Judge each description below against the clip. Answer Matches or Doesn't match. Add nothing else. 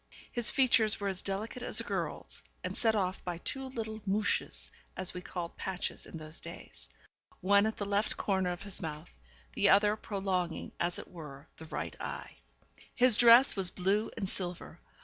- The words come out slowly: Doesn't match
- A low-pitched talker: Doesn't match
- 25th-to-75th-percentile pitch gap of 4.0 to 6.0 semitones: Doesn't match